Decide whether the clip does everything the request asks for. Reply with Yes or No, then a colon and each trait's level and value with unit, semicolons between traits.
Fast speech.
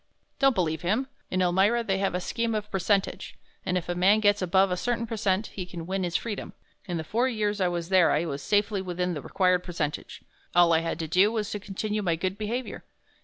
Yes: fast, 225 wpm